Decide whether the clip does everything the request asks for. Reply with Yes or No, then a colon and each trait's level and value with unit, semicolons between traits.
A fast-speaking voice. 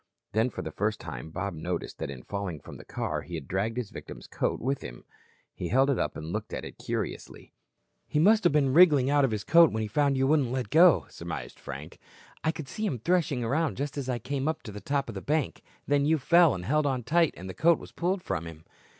Yes: fast, 250 wpm